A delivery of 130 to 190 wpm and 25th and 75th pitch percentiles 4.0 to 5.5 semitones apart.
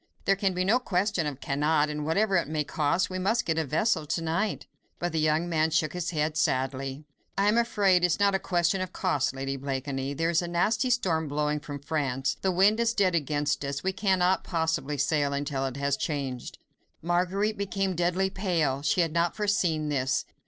No: fast, 205 wpm; average, 4.5 semitones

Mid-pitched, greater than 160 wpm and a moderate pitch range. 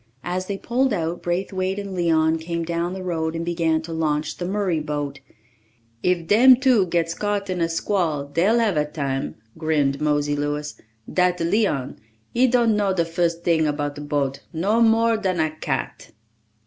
Yes: medium, 170 Hz; average, 175 wpm; average, 3.8 semitones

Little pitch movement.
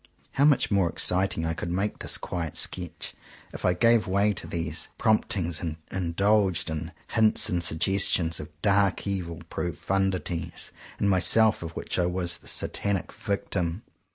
No: average, 3.0 semitones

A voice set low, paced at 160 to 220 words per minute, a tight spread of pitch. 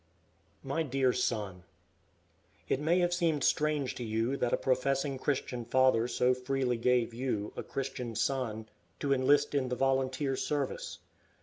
No: low, 130 Hz; average, 145 wpm; narrow, 2.1 semitones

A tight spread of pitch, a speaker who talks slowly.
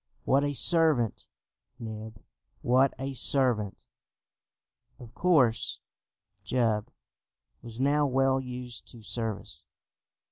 No: average, 3.2 semitones; slow, 95 wpm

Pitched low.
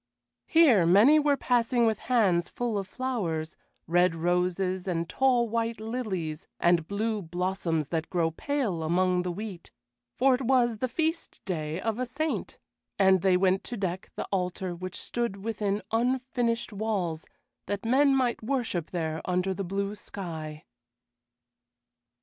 No: high, 195 Hz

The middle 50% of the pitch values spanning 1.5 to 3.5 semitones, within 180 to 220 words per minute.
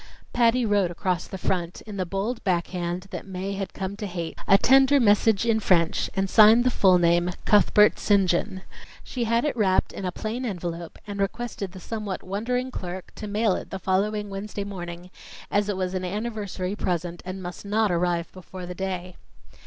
Yes: average, 2.8 semitones; average, 190 wpm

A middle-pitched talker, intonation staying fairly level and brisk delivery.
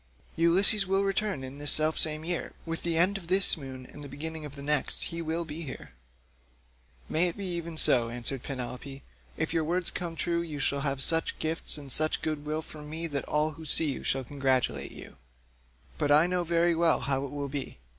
No: medium, 155 Hz; average, 3.1 semitones; fast, 215 wpm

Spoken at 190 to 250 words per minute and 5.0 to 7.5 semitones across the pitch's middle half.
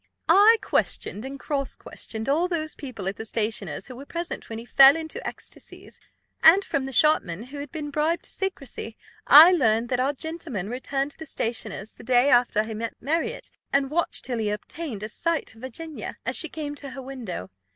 Yes: average, 200 wpm; wide, 5.6 semitones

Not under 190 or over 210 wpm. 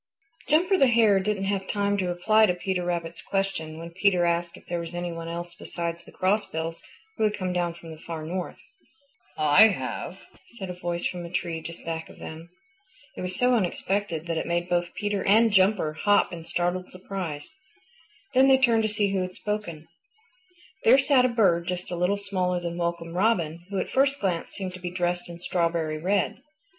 Yes: average, 200 wpm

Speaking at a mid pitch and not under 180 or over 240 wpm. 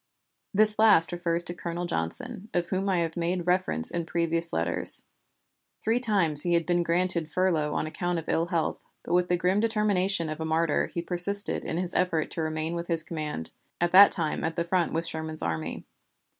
Yes: medium, 170 Hz; average, 200 wpm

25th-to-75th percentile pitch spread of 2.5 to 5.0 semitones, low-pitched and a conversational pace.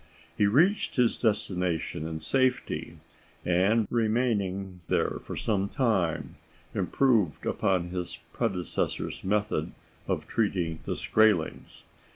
No: average, 4.3 semitones; low, 100 Hz; slow, 105 wpm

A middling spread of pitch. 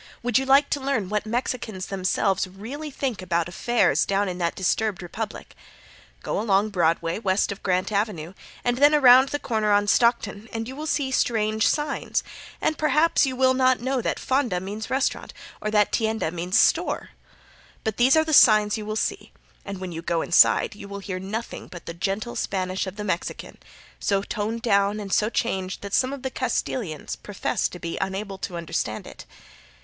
Yes: average, 4.6 semitones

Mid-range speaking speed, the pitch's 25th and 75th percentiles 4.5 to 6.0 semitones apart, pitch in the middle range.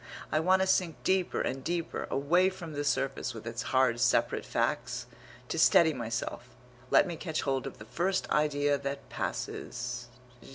Yes: average, 165 wpm; average, 5.2 semitones; medium, 145 Hz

